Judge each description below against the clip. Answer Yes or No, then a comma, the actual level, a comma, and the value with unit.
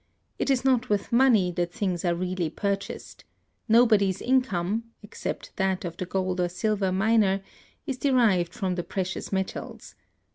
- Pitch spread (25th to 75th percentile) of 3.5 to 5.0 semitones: Yes, average, 3.8 semitones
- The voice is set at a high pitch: Yes, high, 195 Hz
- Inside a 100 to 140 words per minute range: No, average, 150 wpm